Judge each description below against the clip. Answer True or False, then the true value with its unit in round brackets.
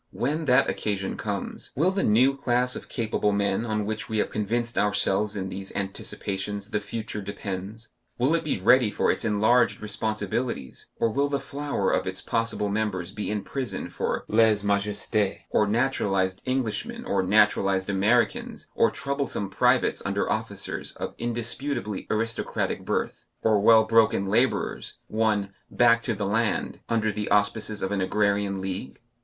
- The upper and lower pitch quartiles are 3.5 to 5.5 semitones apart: False (2.8 semitones)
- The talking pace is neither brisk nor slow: True (155 wpm)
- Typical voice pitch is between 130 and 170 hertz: False (105 Hz)